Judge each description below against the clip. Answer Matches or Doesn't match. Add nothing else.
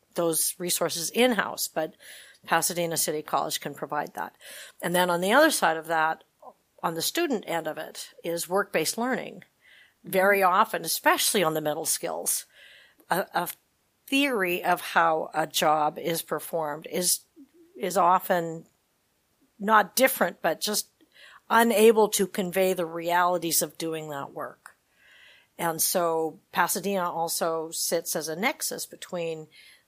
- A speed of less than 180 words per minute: Matches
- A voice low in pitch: Doesn't match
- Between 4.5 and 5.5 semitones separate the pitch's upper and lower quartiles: Doesn't match